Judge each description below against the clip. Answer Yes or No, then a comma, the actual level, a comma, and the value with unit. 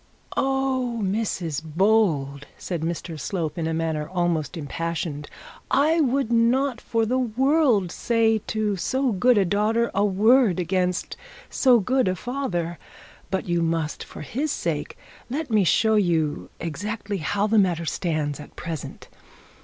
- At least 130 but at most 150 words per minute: Yes, average, 145 wpm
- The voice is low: No, high, 195 Hz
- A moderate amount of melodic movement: No, wide, 6.0 semitones